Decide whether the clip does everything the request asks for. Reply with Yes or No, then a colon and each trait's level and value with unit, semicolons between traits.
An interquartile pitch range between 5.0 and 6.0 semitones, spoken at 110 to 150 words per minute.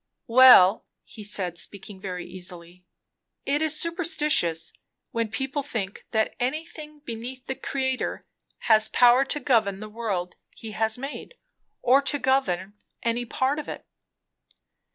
Yes: average, 5.3 semitones; slow, 135 wpm